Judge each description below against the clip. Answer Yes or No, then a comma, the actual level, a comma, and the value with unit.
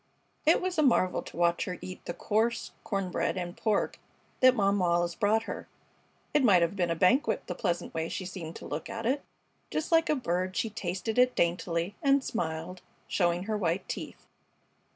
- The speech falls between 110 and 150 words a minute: No, average, 195 wpm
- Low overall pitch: No, high, 190 Hz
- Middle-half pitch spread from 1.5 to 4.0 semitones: No, average, 5.1 semitones